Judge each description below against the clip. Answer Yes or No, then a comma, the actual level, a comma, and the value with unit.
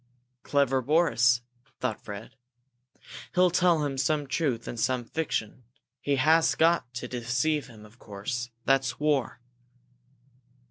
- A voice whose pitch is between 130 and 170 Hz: Yes, low, 135 Hz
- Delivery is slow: Yes, slow, 125 wpm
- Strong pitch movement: No, average, 4.3 semitones